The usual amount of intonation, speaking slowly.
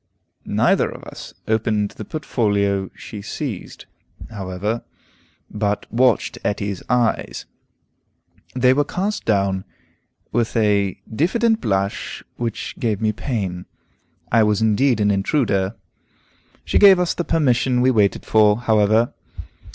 Yes: average, 3.7 semitones; slow, 120 wpm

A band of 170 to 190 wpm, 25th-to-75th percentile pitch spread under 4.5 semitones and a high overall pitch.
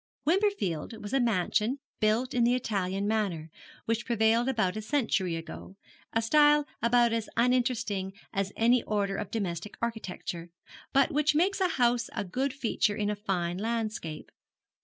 No: average, 155 wpm; average, 4.1 semitones; high, 225 Hz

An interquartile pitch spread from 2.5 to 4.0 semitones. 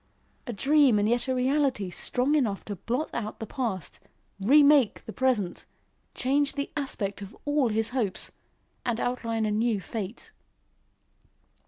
No: average, 4.4 semitones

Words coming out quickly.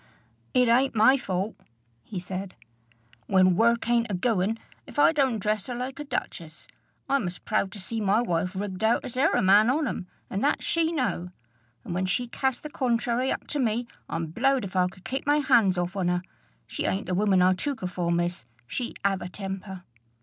Yes: fast, 210 wpm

